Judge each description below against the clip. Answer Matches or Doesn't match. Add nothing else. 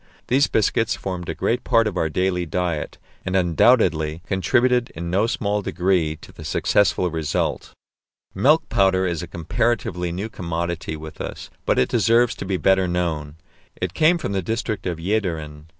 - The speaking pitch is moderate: Doesn't match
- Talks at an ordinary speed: Matches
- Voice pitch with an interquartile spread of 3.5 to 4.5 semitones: Matches